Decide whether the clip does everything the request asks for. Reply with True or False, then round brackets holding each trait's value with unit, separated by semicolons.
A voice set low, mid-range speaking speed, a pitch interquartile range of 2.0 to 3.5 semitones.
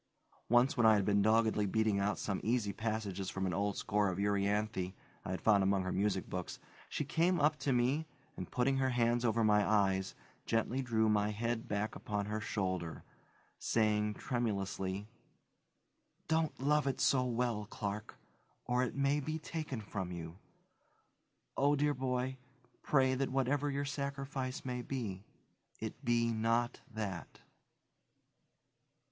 False (110 Hz; 150 wpm; 4.4 semitones)